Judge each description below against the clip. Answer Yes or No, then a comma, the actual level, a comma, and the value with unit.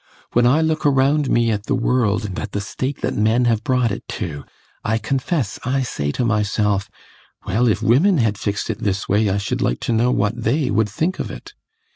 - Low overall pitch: Yes, low, 115 Hz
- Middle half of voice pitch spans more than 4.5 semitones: No, average, 3.9 semitones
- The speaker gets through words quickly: Yes, fast, 215 wpm